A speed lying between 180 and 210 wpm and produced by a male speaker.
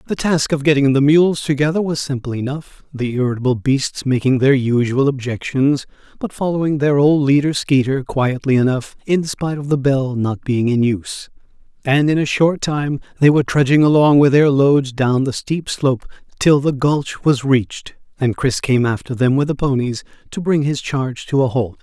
Yes: average, 190 wpm; male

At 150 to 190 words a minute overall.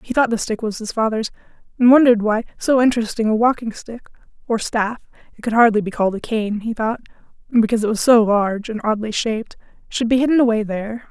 No: average, 200 wpm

